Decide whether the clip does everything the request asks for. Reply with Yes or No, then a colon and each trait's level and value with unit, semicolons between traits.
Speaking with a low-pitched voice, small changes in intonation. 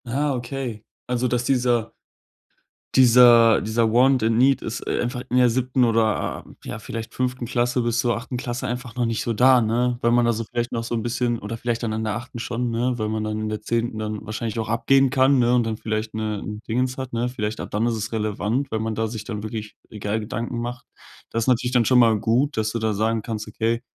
Yes: low, 115 Hz; narrow, 2.0 semitones